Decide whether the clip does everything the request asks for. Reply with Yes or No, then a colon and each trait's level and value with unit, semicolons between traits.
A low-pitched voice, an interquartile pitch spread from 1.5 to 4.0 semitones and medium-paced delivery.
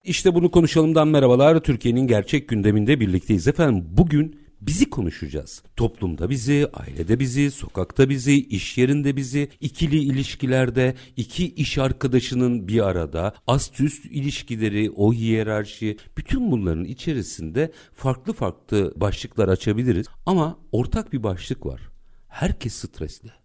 No: low, 125 Hz; average, 5.3 semitones; average, 120 wpm